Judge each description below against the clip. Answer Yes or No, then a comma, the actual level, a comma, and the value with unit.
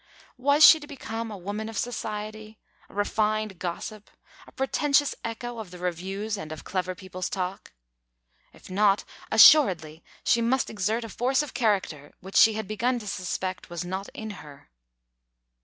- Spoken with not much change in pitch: No, average, 3.8 semitones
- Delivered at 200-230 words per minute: No, average, 160 wpm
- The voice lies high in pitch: Yes, high, 210 Hz